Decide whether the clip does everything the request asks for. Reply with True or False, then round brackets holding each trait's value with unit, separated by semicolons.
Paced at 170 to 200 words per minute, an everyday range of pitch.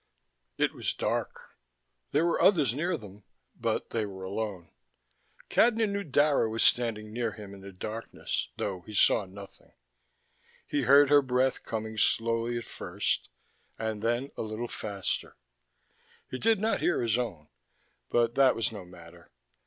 False (155 wpm; 4.7 semitones)